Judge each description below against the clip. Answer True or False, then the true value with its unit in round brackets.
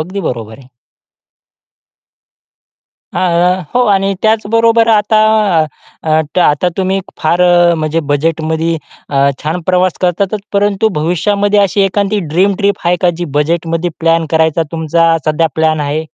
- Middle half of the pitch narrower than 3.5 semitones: False (3.8 semitones)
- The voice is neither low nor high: True (175 Hz)